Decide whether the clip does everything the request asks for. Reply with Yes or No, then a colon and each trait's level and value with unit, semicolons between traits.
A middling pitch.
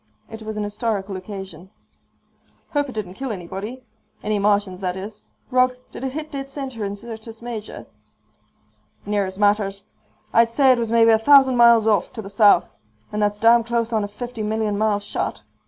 No: high, 220 Hz